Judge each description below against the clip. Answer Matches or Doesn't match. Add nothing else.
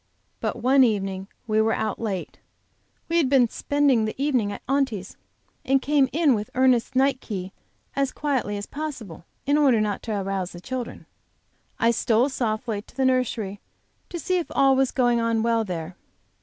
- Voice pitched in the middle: Doesn't match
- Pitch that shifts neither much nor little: Matches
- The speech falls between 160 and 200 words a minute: Matches